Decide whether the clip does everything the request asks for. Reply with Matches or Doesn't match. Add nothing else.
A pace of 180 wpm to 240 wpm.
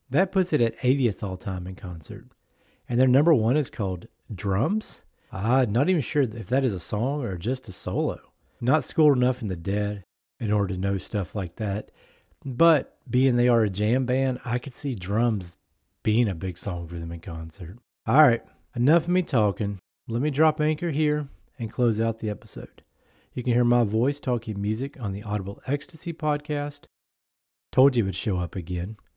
Matches